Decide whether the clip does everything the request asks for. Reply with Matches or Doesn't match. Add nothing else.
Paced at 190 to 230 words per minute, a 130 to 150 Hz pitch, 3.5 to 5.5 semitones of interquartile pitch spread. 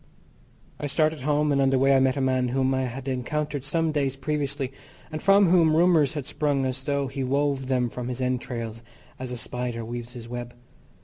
Doesn't match